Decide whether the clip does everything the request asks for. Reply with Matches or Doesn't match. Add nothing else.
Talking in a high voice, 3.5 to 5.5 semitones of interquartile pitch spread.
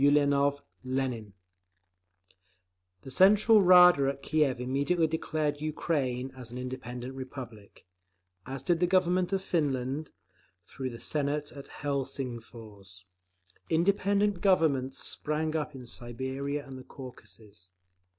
Doesn't match